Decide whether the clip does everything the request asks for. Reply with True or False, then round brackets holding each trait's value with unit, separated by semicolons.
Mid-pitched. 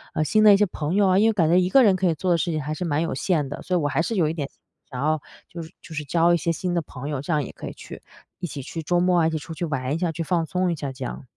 True (165 Hz)